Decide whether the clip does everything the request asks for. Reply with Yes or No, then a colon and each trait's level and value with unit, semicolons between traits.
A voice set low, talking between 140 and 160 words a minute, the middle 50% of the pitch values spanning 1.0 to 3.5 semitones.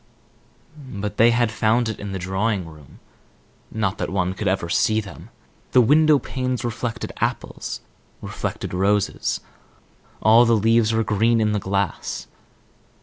Yes: low, 110 Hz; average, 145 wpm; average, 3.1 semitones